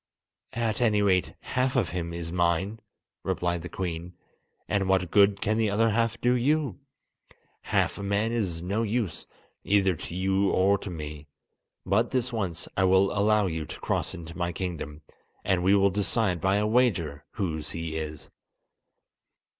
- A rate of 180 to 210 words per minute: No, average, 165 wpm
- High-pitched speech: No, very low, 95 Hz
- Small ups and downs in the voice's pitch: No, average, 3.9 semitones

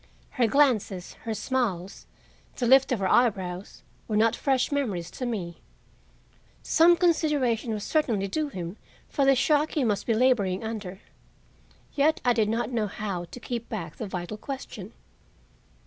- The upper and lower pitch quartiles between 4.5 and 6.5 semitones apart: Yes, average, 5.2 semitones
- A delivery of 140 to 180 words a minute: Yes, average, 155 wpm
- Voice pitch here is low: No, high, 230 Hz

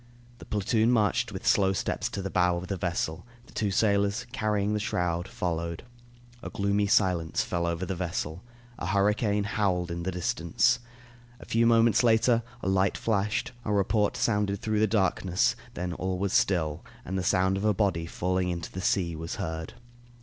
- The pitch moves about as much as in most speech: Yes, average, 3.0 semitones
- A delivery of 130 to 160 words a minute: No, average, 180 wpm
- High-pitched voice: No, very low, 95 Hz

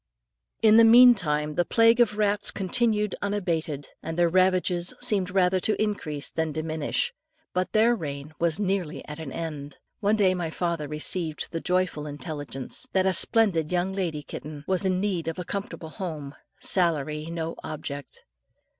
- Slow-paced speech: No, average, 160 wpm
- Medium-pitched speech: Yes, medium, 175 Hz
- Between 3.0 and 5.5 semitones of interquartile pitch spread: Yes, average, 4.4 semitones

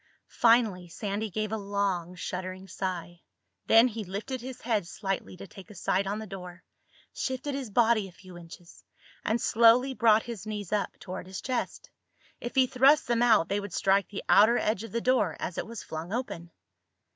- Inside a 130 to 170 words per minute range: No, average, 190 wpm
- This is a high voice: Yes, high, 205 Hz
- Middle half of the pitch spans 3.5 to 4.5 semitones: Yes, average, 4.0 semitones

